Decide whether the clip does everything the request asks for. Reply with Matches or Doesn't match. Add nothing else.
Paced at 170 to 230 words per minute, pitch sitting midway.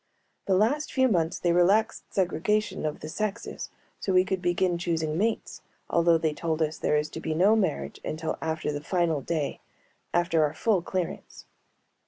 Matches